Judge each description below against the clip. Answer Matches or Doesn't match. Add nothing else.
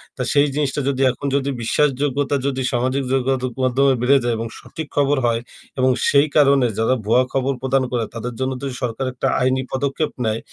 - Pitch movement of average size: Doesn't match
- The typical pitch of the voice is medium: Doesn't match